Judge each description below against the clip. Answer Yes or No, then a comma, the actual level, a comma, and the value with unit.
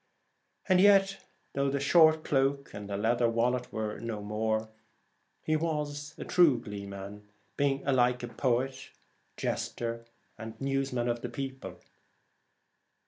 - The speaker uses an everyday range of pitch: Yes, average, 3.9 semitones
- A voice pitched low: Yes, low, 125 Hz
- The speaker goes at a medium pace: No, slow, 125 wpm